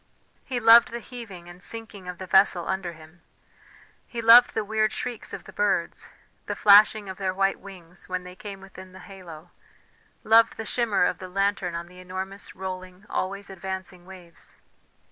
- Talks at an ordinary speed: Yes, average, 175 wpm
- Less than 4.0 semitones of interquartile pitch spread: Yes, narrow, 2.6 semitones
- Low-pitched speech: No, high, 190 Hz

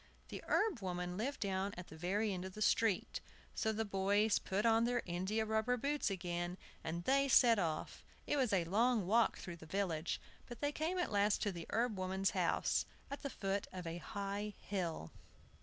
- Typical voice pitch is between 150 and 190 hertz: No, high, 200 Hz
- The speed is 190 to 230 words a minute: Yes, average, 195 wpm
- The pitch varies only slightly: No, average, 3.9 semitones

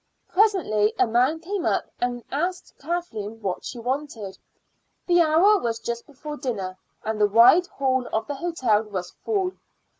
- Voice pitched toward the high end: Yes, very high, 260 Hz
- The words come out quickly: No, average, 155 wpm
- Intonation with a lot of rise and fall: Yes, wide, 7.5 semitones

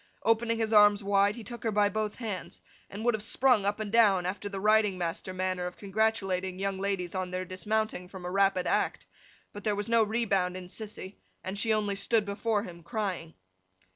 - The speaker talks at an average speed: No, fast, 210 wpm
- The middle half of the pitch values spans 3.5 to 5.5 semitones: No, average, 2.7 semitones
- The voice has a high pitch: Yes, high, 205 Hz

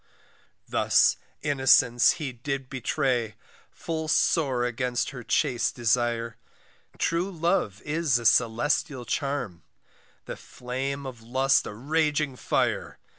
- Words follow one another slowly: Yes, slow, 110 wpm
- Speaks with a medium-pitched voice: No, low, 130 Hz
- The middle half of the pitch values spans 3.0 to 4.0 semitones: Yes, average, 3.6 semitones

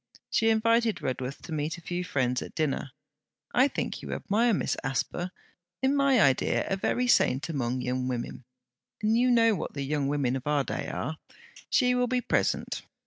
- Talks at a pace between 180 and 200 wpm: Yes, average, 185 wpm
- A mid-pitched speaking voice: Yes, medium, 165 Hz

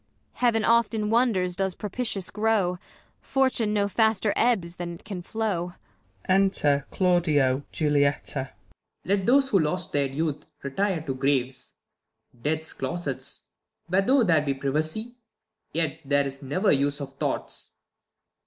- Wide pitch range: Yes, wide, 6.6 semitones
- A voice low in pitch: No, medium, 175 Hz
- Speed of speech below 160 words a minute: Yes, slow, 135 wpm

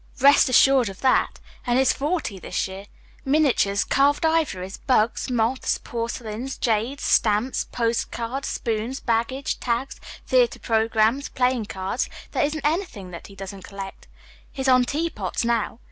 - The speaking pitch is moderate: No, high, 240 Hz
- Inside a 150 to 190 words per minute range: No, slow, 135 wpm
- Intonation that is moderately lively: Yes, average, 4.2 semitones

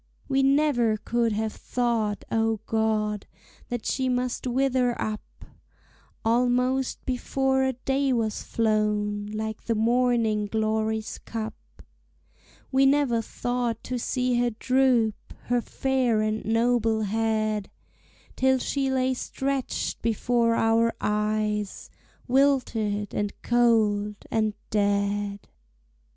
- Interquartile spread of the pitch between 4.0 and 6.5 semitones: No, average, 2.7 semitones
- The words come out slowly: Yes, slow, 110 wpm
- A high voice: Yes, high, 230 Hz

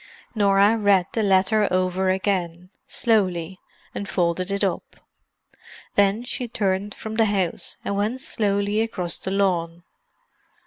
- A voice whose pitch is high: Yes, high, 195 Hz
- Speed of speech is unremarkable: No, slow, 130 wpm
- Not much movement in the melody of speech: Yes, narrow, 2.2 semitones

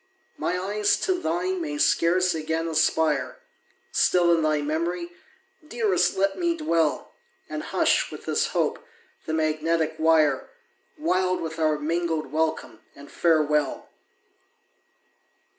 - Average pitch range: Yes, average, 3.1 semitones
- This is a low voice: No, medium, 165 Hz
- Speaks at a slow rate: Yes, slow, 120 wpm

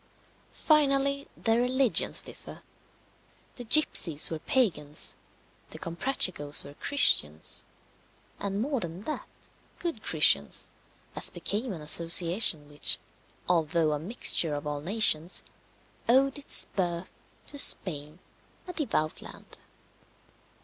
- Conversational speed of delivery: No, slow, 110 wpm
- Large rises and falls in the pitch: Yes, wide, 8.9 semitones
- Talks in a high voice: No, medium, 180 Hz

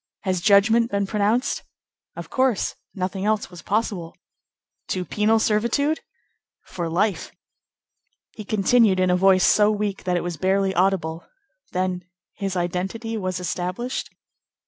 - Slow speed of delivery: Yes, slow, 130 wpm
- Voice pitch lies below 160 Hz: No, high, 195 Hz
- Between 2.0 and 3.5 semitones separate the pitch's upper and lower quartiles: Yes, average, 2.9 semitones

